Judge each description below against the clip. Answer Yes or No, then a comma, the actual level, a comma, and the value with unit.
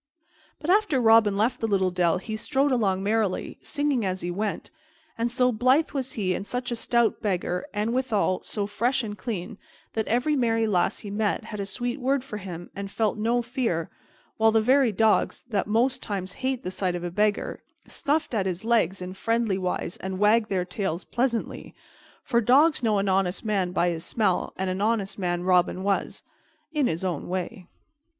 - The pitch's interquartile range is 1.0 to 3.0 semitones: No, average, 4.3 semitones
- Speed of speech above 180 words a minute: Yes, average, 195 wpm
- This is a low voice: No, high, 215 Hz